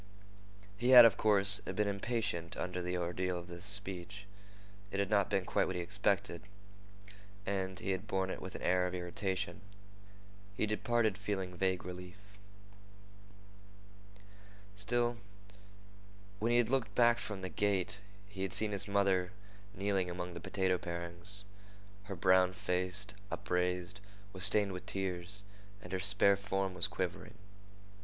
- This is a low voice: Yes, very low, 95 Hz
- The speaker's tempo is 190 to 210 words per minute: No, average, 145 wpm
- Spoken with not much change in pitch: Yes, narrow, 2.1 semitones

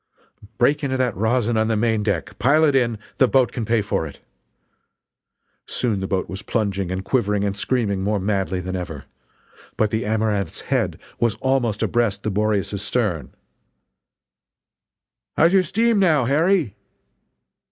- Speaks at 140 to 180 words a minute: Yes, average, 150 wpm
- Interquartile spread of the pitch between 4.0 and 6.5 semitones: Yes, average, 4.3 semitones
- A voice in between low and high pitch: No, low, 110 Hz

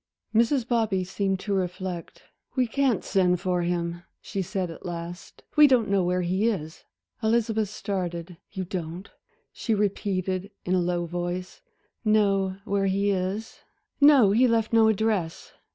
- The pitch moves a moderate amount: Yes, average, 3.6 semitones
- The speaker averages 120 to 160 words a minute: Yes, average, 150 wpm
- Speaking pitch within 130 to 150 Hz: No, high, 195 Hz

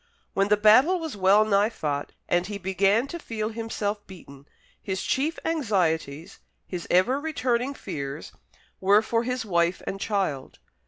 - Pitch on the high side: Yes, high, 205 Hz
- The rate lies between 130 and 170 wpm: Yes, average, 150 wpm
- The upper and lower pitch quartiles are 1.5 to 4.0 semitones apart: No, average, 4.4 semitones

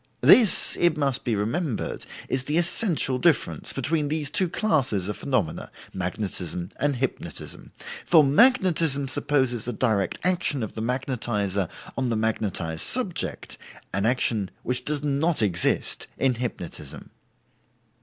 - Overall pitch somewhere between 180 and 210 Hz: No, low, 130 Hz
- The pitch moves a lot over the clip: Yes, wide, 6.2 semitones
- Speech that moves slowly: Yes, slow, 130 wpm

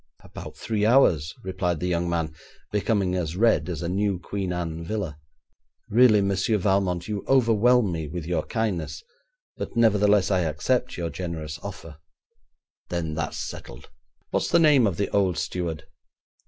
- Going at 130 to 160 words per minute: Yes, average, 155 wpm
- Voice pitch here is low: Yes, very low, 95 Hz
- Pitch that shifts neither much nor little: Yes, average, 3.9 semitones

